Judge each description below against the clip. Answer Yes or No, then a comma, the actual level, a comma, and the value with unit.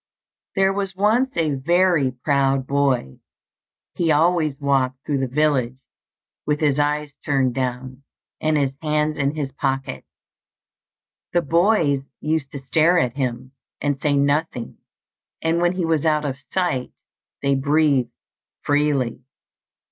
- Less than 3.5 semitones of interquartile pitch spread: Yes, average, 3.1 semitones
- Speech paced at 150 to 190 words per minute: No, slow, 135 wpm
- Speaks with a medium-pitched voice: Yes, medium, 145 Hz